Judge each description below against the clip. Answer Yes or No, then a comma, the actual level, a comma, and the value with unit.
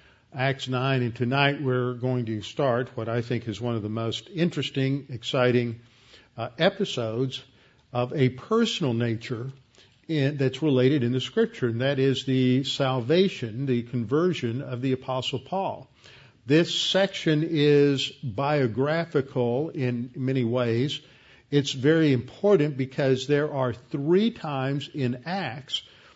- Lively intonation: No, average, 3.0 semitones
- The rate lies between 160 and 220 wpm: No, slow, 135 wpm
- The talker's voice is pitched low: Yes, low, 130 Hz